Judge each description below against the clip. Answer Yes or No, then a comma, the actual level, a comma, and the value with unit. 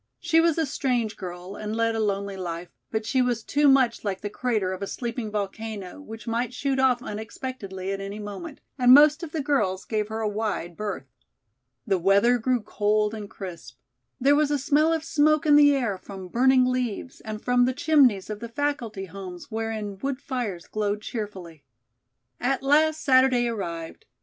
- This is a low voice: No, high, 225 Hz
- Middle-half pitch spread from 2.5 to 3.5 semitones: No, average, 4.8 semitones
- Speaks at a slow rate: No, average, 185 wpm